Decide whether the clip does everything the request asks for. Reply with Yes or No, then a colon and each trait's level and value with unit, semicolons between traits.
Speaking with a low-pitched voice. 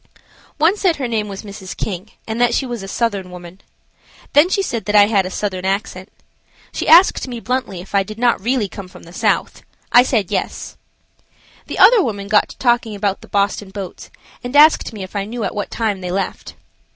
No: high, 210 Hz